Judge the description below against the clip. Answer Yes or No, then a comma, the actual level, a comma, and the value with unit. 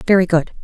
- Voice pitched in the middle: Yes, medium, 180 Hz